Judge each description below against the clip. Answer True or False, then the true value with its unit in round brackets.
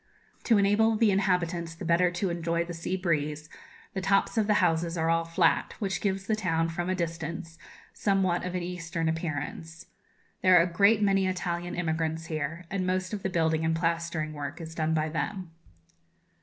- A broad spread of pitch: False (2.5 semitones)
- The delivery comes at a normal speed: True (185 wpm)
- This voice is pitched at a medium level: True (170 Hz)